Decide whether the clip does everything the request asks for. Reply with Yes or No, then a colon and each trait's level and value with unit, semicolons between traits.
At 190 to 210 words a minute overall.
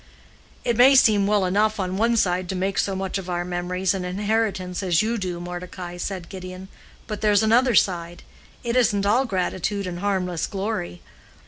No: average, 180 wpm